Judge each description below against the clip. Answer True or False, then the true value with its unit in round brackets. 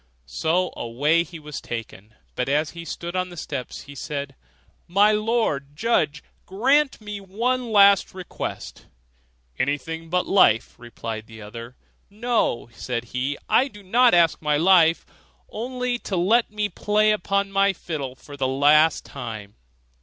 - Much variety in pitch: True (7.1 semitones)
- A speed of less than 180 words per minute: True (150 wpm)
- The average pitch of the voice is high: False (170 Hz)